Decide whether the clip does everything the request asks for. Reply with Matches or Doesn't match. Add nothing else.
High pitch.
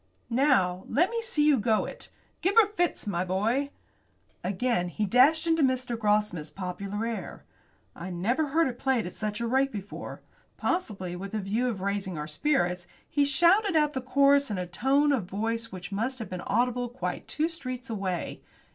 Matches